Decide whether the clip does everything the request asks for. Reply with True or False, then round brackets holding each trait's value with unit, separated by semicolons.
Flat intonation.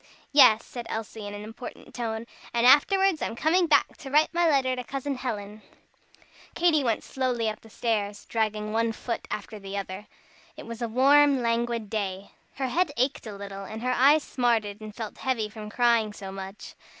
False (3.8 semitones)